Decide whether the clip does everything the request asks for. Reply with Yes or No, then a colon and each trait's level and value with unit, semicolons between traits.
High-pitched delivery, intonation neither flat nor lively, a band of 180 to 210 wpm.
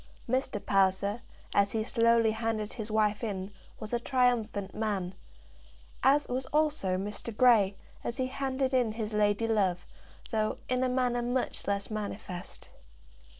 No: high, 220 Hz; average, 3.4 semitones; average, 145 wpm